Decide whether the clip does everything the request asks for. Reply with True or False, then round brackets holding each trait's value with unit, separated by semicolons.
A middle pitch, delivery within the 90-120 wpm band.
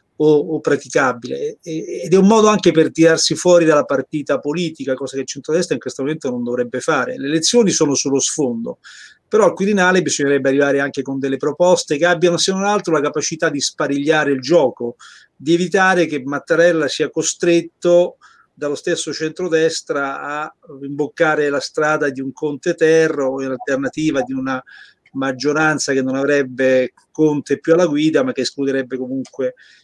False (150 Hz; 165 wpm)